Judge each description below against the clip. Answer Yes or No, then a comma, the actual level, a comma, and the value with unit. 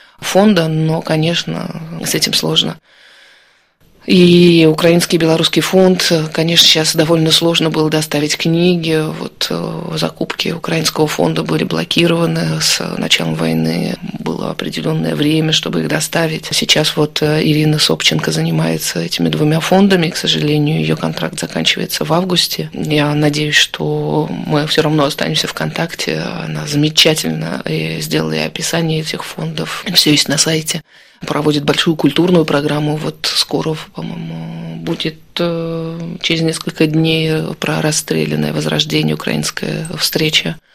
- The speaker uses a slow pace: No, average, 120 wpm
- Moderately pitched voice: Yes, medium, 155 Hz